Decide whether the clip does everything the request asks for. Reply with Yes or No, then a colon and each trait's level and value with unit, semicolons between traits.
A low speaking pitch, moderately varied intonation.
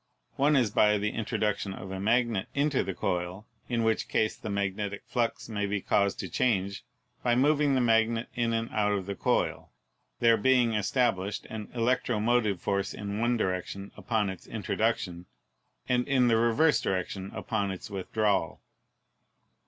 Yes: low, 110 Hz; average, 3.2 semitones